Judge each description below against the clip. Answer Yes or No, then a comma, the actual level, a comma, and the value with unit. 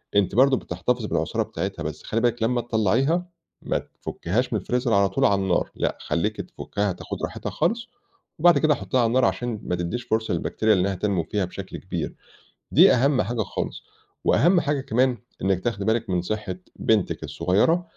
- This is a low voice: Yes, low, 110 Hz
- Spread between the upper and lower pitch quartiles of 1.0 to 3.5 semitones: No, average, 4.8 semitones